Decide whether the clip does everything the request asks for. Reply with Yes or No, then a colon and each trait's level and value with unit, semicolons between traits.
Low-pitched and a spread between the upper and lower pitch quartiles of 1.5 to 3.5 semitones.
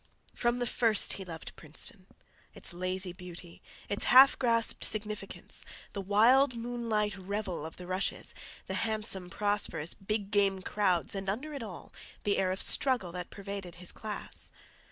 No: high, 200 Hz; average, 3.2 semitones